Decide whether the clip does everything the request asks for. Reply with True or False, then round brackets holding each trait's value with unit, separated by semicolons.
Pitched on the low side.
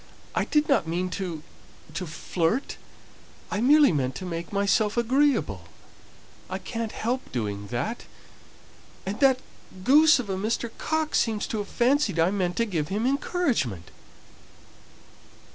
False (205 Hz)